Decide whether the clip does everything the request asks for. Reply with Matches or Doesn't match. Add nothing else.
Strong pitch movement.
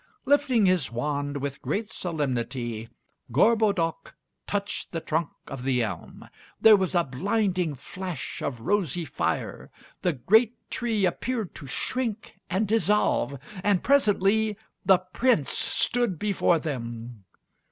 Matches